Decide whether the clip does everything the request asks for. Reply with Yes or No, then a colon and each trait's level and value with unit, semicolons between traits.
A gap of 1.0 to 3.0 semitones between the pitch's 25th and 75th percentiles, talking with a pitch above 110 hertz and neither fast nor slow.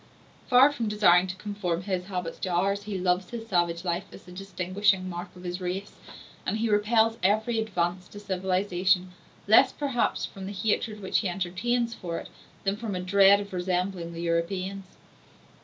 Yes: narrow, 2.5 semitones; high, 190 Hz; average, 175 wpm